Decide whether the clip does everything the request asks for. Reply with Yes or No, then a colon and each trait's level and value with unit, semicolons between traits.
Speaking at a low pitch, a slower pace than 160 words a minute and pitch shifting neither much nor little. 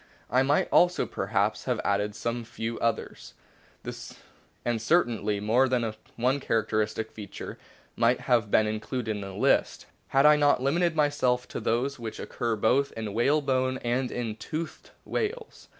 Yes: low, 120 Hz; average, 150 wpm; average, 3.7 semitones